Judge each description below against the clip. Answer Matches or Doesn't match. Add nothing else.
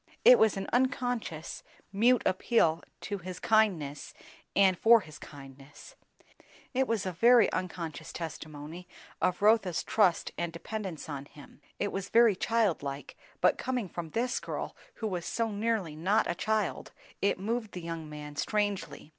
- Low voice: Doesn't match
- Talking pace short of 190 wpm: Matches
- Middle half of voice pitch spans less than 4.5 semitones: Doesn't match